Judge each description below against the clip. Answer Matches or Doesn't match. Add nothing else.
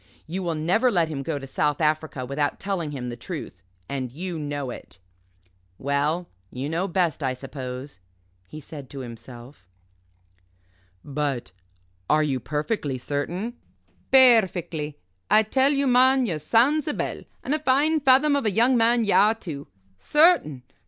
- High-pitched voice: Doesn't match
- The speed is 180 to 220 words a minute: Doesn't match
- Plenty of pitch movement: Matches